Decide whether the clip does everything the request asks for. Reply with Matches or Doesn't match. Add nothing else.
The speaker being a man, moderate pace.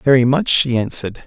Matches